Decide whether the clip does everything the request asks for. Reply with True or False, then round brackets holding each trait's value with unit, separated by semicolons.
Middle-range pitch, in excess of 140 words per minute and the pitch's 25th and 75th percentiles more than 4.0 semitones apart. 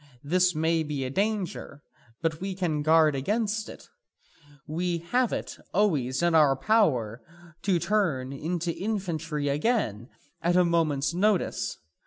False (165 Hz; 135 wpm; 4.7 semitones)